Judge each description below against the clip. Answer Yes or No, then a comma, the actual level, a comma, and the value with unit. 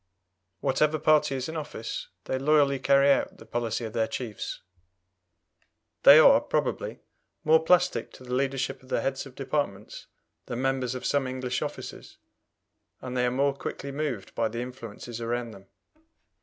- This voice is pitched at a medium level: No, low, 130 Hz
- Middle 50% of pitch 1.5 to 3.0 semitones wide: Yes, narrow, 2.6 semitones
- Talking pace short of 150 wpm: No, average, 160 wpm